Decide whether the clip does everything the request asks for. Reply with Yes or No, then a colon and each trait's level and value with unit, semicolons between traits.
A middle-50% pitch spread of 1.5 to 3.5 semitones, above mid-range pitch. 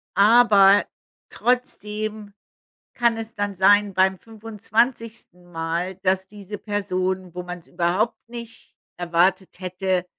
Yes: average, 2.9 semitones; high, 200 Hz